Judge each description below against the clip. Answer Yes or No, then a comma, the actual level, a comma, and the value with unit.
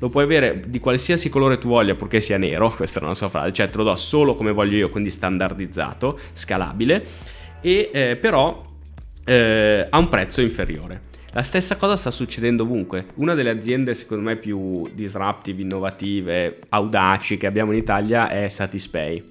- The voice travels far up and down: No, average, 4.2 semitones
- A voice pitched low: Yes, low, 105 Hz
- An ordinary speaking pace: No, fast, 175 wpm